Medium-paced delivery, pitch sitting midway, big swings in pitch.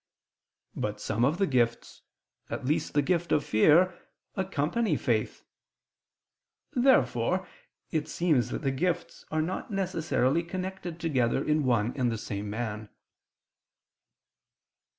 No: slow, 120 wpm; medium, 150 Hz; wide, 6.5 semitones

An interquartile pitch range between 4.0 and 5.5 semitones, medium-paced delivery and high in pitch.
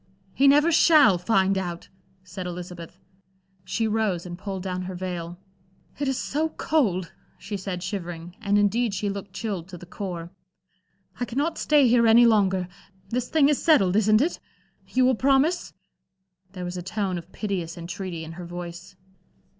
Yes: average, 4.9 semitones; average, 165 wpm; high, 195 Hz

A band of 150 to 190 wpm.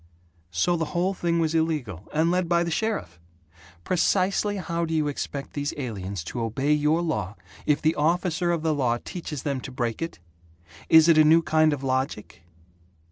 Yes: average, 185 wpm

